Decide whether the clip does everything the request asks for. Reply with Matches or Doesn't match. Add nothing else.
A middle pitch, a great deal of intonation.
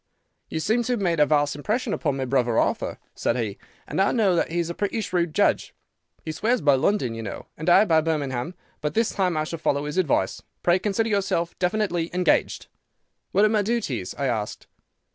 Matches